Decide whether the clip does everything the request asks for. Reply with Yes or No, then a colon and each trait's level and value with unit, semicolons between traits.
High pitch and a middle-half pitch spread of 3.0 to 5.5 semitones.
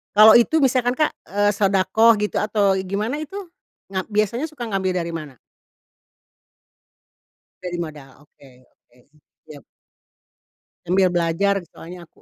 Yes: high, 195 Hz; average, 4.2 semitones